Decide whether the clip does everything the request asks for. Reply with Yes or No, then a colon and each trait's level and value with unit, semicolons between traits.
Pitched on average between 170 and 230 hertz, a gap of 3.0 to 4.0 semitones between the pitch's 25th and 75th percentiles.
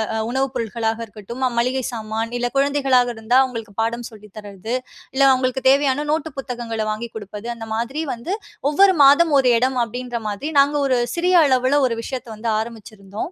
No: high, 245 Hz; average, 3.3 semitones